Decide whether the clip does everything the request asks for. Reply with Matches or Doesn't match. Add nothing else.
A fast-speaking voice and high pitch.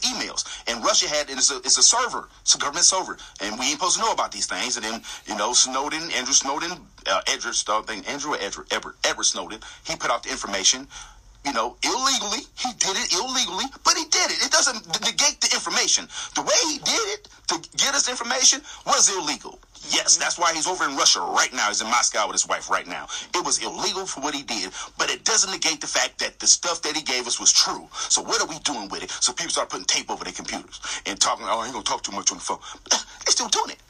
Matches